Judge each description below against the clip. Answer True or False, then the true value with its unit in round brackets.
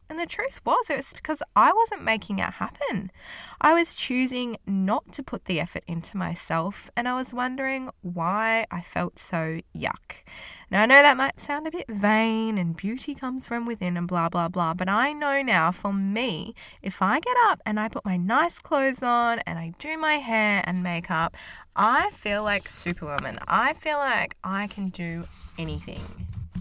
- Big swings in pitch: True (7.2 semitones)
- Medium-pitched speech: False (215 Hz)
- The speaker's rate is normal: True (190 wpm)